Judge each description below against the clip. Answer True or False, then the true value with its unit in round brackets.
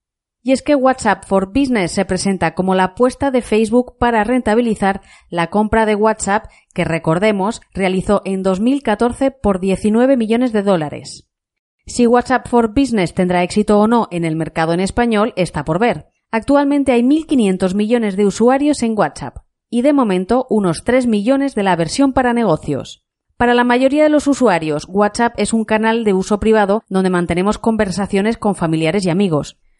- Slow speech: False (170 wpm)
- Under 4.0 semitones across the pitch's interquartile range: False (4.4 semitones)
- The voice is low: False (215 Hz)